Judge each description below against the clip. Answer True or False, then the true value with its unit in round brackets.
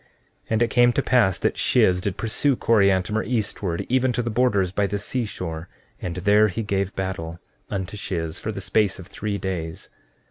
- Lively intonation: False (3.6 semitones)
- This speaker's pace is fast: False (185 wpm)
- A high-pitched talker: False (100 Hz)